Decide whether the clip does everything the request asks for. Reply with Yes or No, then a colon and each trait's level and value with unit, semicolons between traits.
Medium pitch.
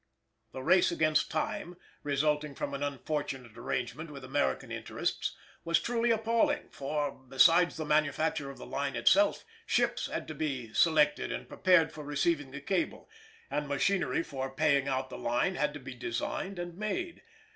Yes: medium, 150 Hz